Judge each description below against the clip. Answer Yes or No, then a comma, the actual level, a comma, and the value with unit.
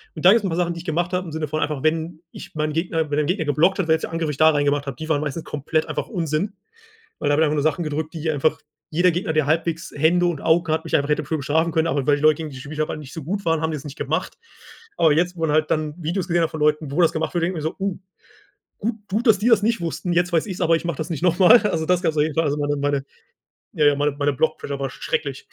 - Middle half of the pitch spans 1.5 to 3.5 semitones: Yes, narrow, 2.5 semitones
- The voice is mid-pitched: Yes, medium, 160 Hz